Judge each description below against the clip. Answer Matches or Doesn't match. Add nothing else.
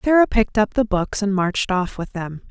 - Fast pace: Matches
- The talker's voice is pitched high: Matches